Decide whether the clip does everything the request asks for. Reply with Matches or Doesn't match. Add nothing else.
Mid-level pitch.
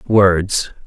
Doesn't match